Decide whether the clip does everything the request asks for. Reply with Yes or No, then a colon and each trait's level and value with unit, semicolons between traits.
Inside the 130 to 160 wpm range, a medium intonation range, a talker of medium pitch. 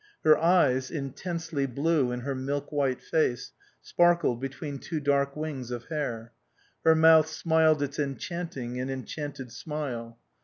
Yes: average, 140 wpm; average, 3.5 semitones; medium, 145 Hz